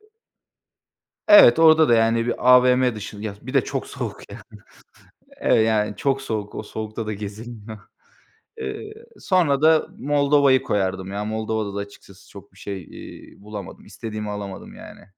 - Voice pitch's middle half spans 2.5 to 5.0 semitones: Yes, average, 4.7 semitones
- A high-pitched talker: No, low, 110 Hz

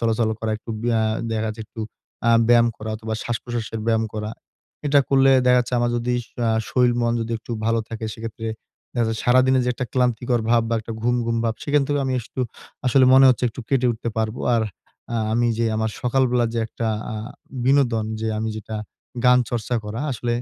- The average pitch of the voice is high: No, low, 120 Hz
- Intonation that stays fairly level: Yes, narrow, 1.9 semitones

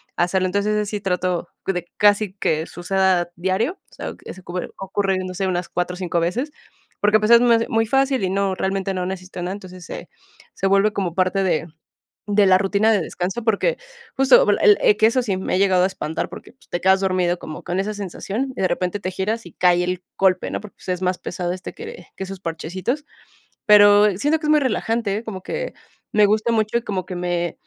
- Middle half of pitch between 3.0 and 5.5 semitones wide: No, narrow, 2.6 semitones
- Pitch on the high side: Yes, high, 195 Hz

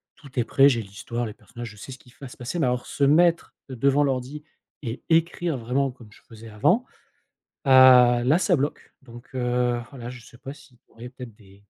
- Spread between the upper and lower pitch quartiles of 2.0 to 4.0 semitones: Yes, average, 2.8 semitones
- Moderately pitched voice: No, low, 125 Hz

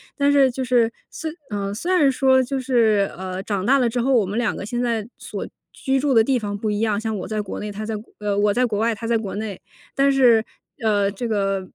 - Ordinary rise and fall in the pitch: Yes, average, 3.7 semitones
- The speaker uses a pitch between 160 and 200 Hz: No, high, 225 Hz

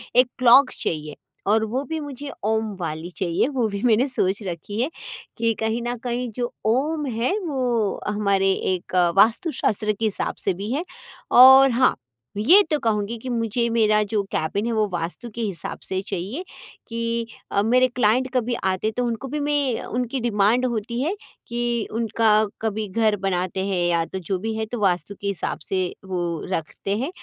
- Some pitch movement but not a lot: Yes, average, 3.9 semitones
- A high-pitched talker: Yes, high, 225 Hz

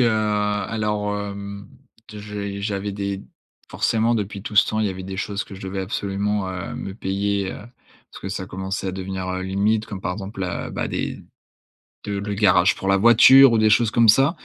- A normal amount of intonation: No, narrow, 1.6 semitones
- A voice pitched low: Yes, low, 100 Hz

